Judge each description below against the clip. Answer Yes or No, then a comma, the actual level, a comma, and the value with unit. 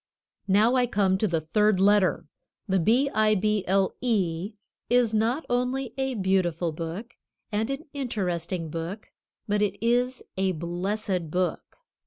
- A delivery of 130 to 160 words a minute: Yes, average, 145 wpm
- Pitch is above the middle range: Yes, high, 205 Hz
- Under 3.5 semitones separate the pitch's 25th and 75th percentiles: No, average, 4.4 semitones